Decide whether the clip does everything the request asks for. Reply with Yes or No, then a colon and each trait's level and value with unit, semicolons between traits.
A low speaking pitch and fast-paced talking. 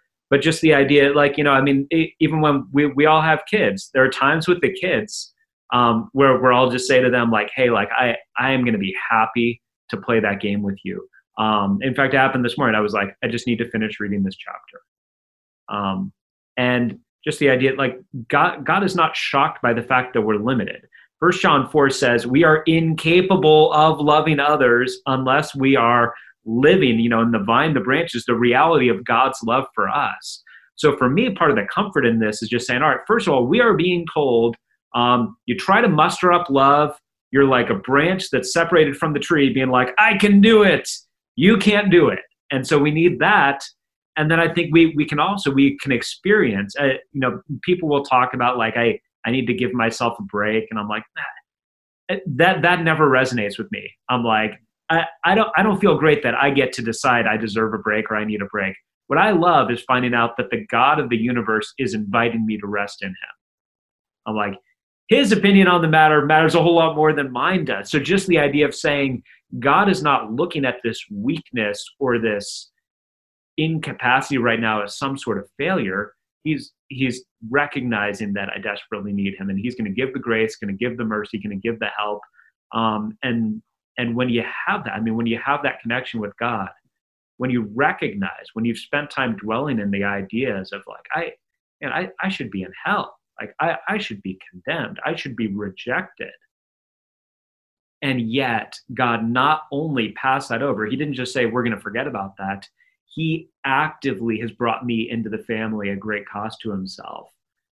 Yes: low, 130 Hz; fast, 210 wpm